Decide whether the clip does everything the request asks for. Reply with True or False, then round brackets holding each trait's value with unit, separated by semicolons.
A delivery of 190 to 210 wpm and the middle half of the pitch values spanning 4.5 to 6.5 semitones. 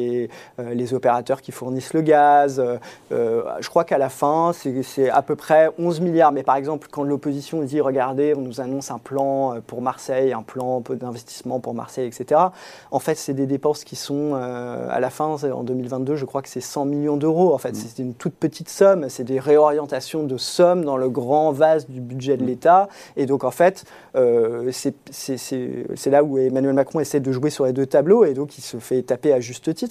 False (205 wpm; 2.9 semitones)